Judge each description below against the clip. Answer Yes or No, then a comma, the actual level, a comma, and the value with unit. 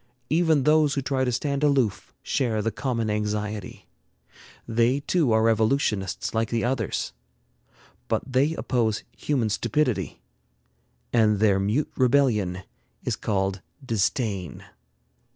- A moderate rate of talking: No, slow, 115 wpm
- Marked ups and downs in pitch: No, average, 4.4 semitones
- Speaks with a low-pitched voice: Yes, low, 115 Hz